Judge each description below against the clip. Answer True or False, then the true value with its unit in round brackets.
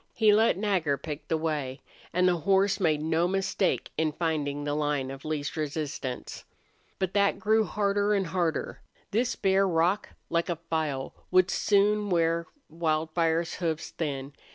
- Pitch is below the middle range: False (165 Hz)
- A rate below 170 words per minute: True (155 wpm)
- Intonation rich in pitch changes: False (4.0 semitones)